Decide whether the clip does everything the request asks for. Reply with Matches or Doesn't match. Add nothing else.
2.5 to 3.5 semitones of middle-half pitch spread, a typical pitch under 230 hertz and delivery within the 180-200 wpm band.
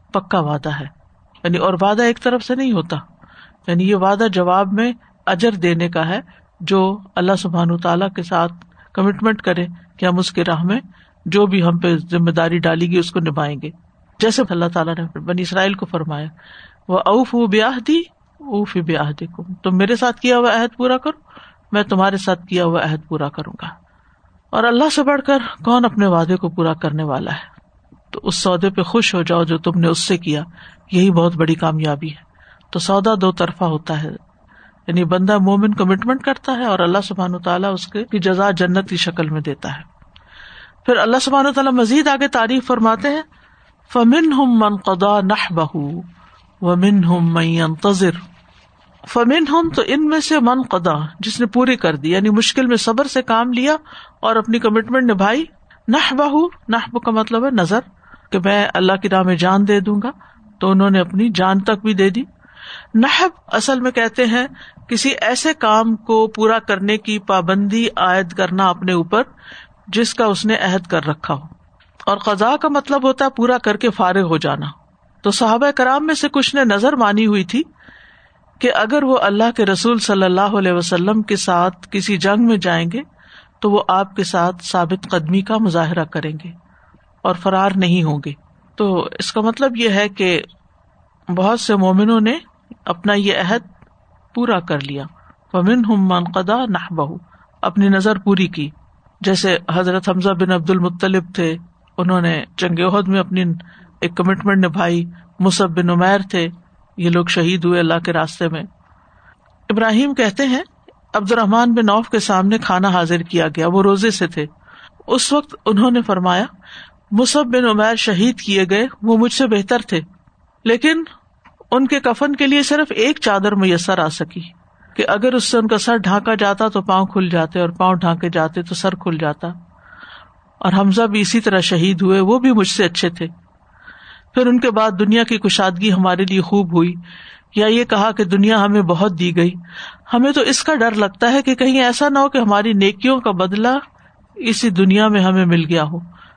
Doesn't match